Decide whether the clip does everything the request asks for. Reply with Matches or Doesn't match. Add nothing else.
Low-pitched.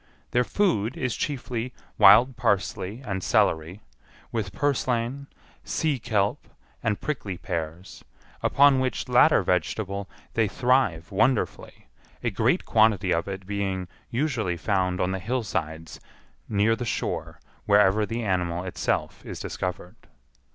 Matches